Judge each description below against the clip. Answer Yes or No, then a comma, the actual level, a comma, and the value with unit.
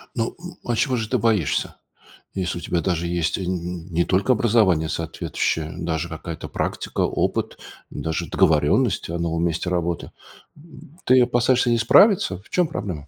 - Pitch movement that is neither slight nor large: No, wide, 6.3 semitones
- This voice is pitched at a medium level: No, very low, 95 Hz